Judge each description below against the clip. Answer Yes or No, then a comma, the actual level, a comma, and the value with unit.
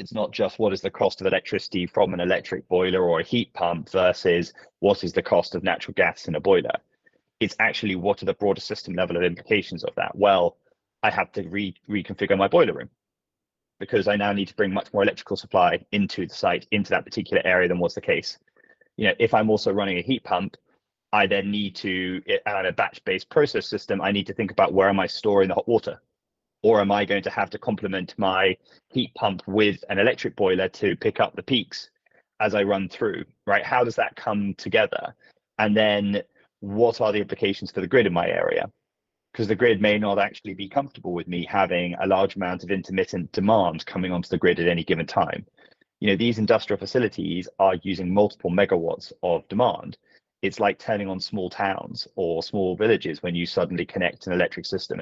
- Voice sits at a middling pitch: No, low, 100 Hz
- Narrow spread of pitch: Yes, narrow, 2.1 semitones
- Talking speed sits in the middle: No, fast, 210 wpm